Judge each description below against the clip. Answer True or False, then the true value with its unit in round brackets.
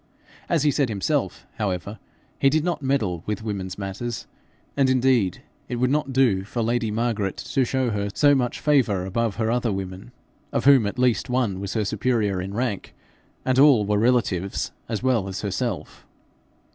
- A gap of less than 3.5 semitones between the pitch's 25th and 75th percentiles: False (4.5 semitones)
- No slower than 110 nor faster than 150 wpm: False (175 wpm)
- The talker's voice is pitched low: True (115 Hz)